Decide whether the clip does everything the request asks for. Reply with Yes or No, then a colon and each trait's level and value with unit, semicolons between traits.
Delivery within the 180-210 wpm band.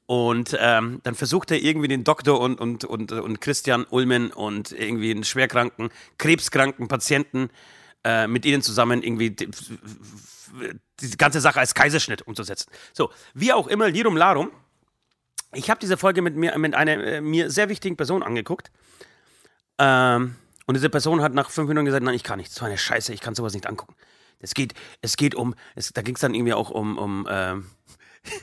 Yes: fast, 190 wpm